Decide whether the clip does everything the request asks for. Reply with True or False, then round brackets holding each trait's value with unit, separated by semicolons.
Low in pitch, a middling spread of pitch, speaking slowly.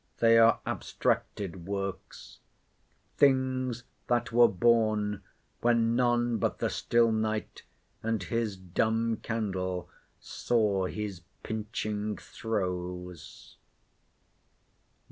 True (110 Hz; 3.1 semitones; 85 wpm)